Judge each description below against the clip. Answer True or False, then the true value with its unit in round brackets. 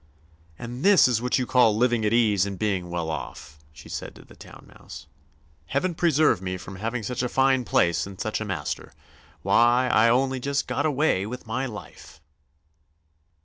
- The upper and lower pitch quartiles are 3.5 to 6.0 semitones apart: True (4.5 semitones)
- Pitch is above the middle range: False (120 Hz)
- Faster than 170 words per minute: True (185 wpm)